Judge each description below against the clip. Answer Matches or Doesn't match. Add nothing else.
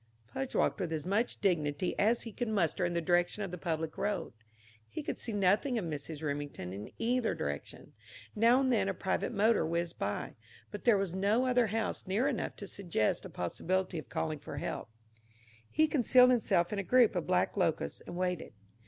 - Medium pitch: Doesn't match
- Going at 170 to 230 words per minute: Matches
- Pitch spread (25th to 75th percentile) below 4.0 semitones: Doesn't match